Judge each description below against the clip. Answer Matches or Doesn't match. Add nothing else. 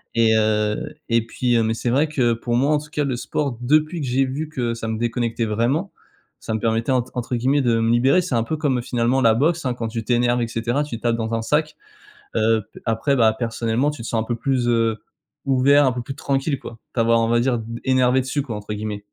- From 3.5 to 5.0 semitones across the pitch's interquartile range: Doesn't match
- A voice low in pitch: Matches